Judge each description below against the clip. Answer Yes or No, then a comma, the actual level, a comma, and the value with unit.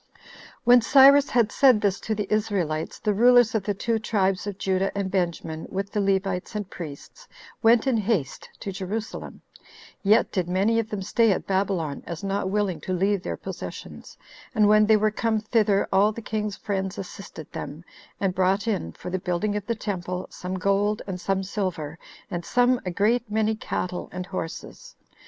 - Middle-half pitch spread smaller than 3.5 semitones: Yes, average, 2.8 semitones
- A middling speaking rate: Yes, average, 185 wpm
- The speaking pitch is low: No, high, 200 Hz